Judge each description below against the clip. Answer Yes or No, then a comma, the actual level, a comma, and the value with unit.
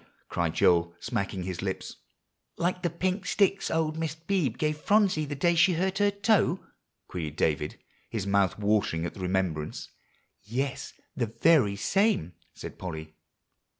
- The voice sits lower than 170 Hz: Yes, low, 135 Hz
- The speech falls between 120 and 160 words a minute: Yes, average, 150 wpm